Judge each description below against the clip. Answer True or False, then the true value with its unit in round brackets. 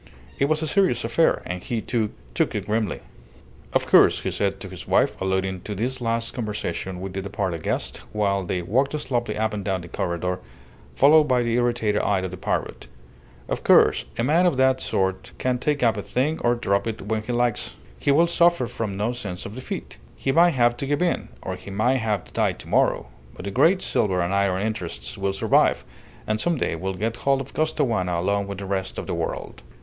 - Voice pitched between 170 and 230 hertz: False (110 Hz)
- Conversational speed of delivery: False (215 wpm)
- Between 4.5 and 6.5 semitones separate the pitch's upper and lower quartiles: True (5.1 semitones)